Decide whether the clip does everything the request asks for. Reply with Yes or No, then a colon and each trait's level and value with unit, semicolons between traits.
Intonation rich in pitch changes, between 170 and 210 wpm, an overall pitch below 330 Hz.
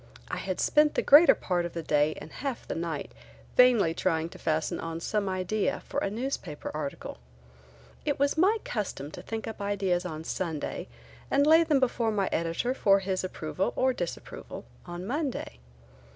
Yes: wide, 7.1 semitones; average, 175 wpm; high, 190 Hz